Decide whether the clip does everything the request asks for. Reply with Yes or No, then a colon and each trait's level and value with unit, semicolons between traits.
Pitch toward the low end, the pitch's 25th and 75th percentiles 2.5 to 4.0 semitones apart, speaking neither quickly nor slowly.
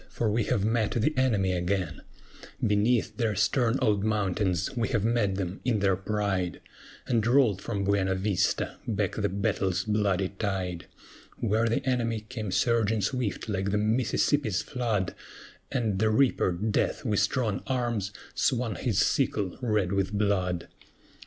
Yes: low, 105 Hz; average, 3.1 semitones; average, 145 wpm